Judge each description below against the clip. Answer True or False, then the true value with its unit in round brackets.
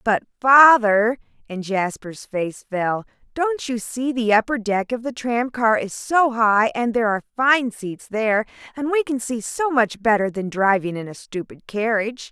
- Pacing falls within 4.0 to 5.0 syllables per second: True (4.5 syllables/s)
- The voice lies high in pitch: True (225 Hz)